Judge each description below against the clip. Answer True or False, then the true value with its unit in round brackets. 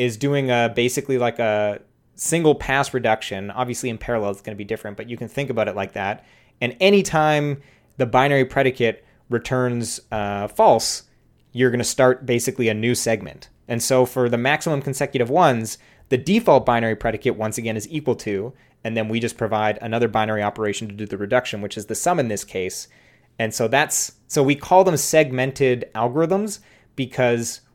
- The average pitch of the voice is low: True (120 Hz)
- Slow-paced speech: False (185 wpm)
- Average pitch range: True (3.4 semitones)